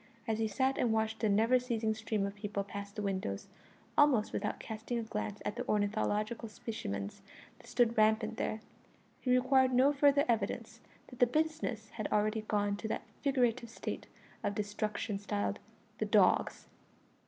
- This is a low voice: No, high, 220 Hz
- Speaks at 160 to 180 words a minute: Yes, average, 165 wpm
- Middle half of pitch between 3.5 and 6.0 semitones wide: No, average, 2.8 semitones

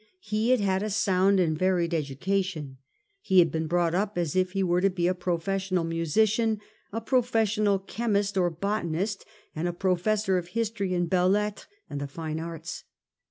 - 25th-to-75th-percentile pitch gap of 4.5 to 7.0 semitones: No, average, 3.3 semitones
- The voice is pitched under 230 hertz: Yes, medium, 185 Hz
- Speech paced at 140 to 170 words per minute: No, average, 180 wpm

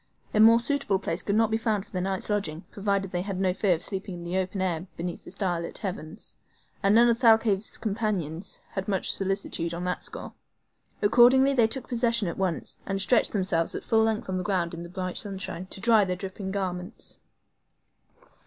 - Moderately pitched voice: No, high, 195 Hz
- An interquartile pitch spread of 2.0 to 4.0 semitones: Yes, average, 3.3 semitones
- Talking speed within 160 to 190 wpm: No, fast, 205 wpm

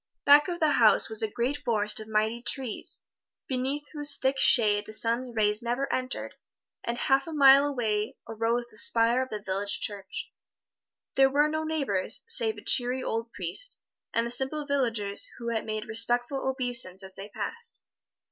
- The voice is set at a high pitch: Yes, high, 240 Hz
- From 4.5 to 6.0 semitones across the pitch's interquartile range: No, average, 4.1 semitones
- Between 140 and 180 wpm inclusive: Yes, average, 170 wpm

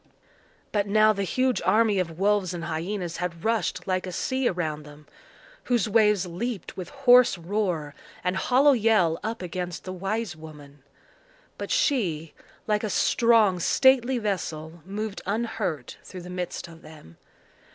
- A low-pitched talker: No, high, 190 Hz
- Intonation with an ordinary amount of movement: Yes, average, 4.7 semitones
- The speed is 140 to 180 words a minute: Yes, average, 150 wpm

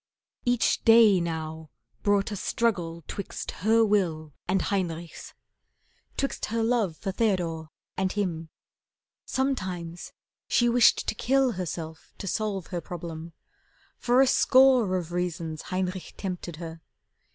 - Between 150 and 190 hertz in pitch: Yes, medium, 185 Hz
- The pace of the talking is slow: Yes, slow, 125 wpm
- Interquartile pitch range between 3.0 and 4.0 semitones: No, average, 5.0 semitones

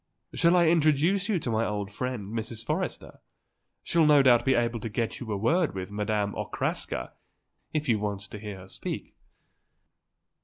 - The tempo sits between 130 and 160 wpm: No, average, 170 wpm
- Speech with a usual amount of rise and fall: No, wide, 6.4 semitones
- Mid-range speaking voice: No, low, 115 Hz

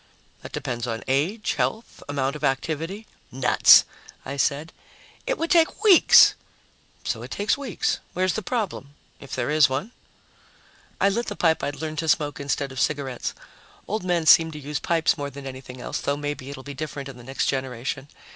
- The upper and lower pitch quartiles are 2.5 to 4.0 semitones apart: No, average, 4.8 semitones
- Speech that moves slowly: No, average, 185 wpm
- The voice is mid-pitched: Yes, medium, 145 Hz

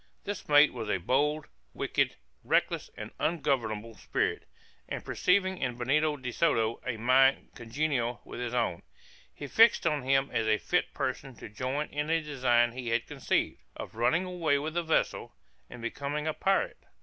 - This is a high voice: No, low, 135 Hz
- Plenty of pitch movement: No, average, 4.4 semitones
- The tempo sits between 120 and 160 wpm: No, average, 170 wpm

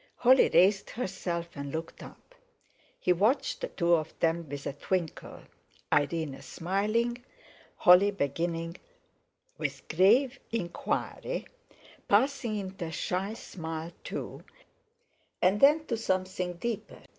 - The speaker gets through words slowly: Yes, slow, 115 wpm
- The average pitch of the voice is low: No, medium, 185 Hz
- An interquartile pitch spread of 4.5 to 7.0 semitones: Yes, average, 5.3 semitones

